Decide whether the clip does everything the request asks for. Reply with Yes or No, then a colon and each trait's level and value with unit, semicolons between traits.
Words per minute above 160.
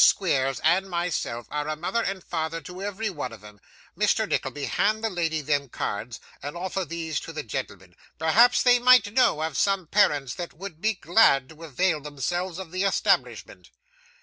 Yes: average, 180 wpm